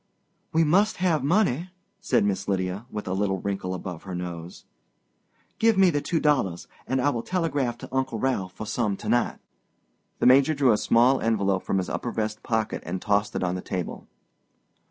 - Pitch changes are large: Yes, wide, 6.9 semitones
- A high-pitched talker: No, low, 115 Hz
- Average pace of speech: Yes, average, 190 wpm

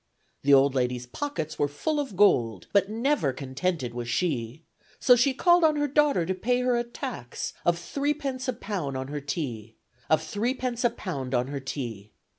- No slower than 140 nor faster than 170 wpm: No, average, 195 wpm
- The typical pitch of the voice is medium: Yes, medium, 170 Hz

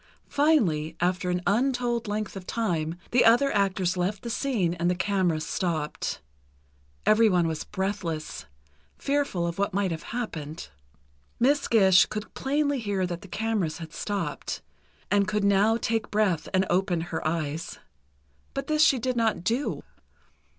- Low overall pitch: No, high, 200 Hz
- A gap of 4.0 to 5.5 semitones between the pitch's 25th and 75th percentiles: Yes, average, 4.9 semitones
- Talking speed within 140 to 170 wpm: Yes, average, 150 wpm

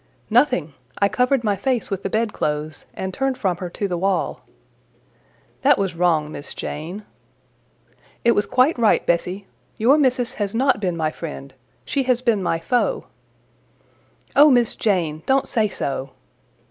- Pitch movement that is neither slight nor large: No, wide, 6.3 semitones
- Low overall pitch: No, high, 200 Hz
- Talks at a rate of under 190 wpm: Yes, average, 155 wpm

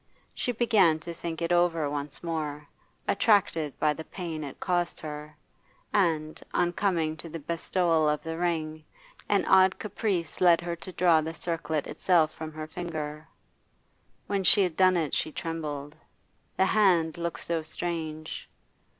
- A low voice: No, medium, 165 Hz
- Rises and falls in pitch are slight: Yes, narrow, 2.2 semitones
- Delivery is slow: No, average, 155 wpm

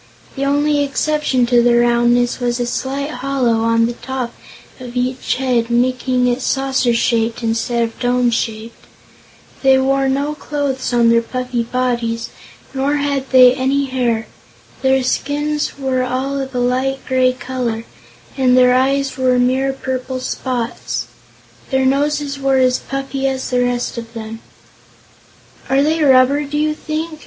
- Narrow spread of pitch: Yes, narrow, 2.0 semitones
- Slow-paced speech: No, average, 150 wpm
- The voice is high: Yes, very high, 255 Hz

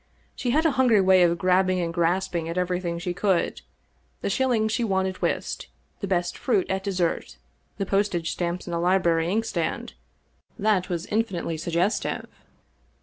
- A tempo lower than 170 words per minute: No, average, 175 wpm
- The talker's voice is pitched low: No, medium, 185 Hz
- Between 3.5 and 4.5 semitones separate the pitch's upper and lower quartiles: No, average, 3.0 semitones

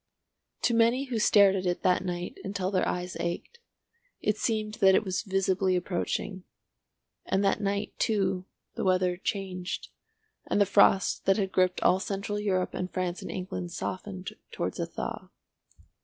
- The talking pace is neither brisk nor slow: Yes, average, 160 wpm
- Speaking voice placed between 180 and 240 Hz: Yes, high, 190 Hz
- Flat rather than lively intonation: Yes, narrow, 1.8 semitones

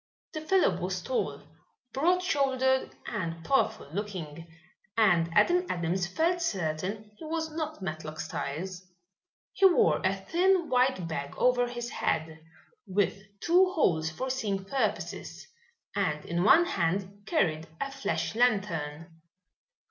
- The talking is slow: Yes, slow, 125 wpm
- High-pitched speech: Yes, high, 205 Hz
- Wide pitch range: Yes, wide, 9.0 semitones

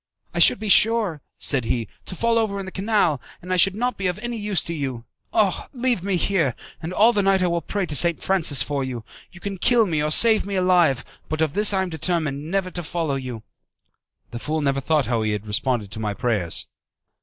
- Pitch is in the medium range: Yes, medium, 170 Hz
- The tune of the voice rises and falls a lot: Yes, wide, 6.4 semitones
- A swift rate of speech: Yes, fast, 235 wpm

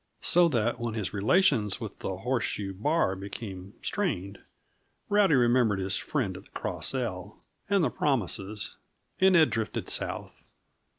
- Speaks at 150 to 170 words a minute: No, average, 140 wpm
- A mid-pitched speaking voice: No, low, 115 Hz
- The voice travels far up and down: Yes, wide, 7.1 semitones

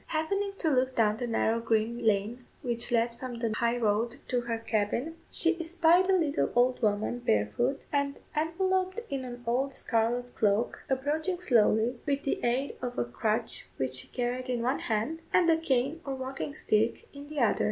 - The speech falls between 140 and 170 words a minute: No, average, 185 wpm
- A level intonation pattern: No, average, 4.2 semitones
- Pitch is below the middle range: No, high, 245 Hz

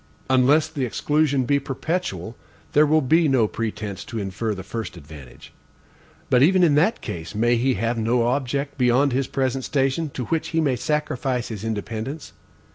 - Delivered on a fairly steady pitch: No, average, 4.4 semitones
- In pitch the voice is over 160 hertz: No, low, 130 Hz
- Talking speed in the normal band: Yes, average, 170 wpm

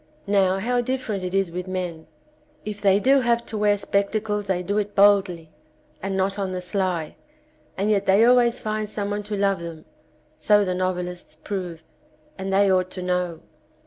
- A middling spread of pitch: No, narrow, 2.3 semitones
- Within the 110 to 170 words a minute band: No, average, 180 wpm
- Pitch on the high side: Yes, high, 195 Hz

